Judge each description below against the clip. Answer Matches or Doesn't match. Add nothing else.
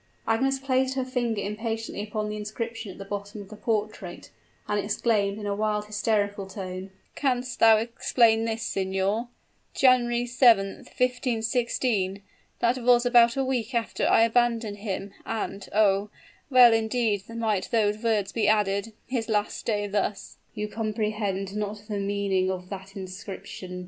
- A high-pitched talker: Matches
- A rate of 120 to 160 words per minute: Matches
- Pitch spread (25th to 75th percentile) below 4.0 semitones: Matches